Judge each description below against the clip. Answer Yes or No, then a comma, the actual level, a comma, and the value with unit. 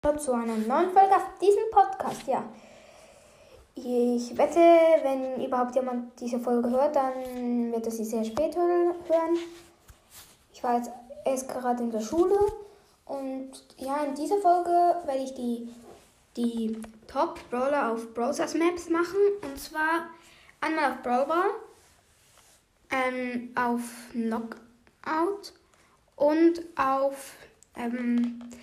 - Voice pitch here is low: No, very high, 275 Hz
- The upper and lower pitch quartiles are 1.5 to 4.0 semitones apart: No, wide, 5.6 semitones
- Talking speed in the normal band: No, slow, 120 wpm